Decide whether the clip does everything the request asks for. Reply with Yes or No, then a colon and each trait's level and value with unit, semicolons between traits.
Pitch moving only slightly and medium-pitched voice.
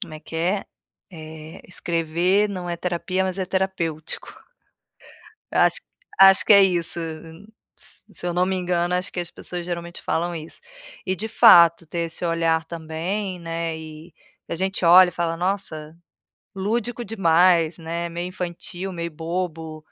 Yes: narrow, 2.2 semitones; medium, 170 Hz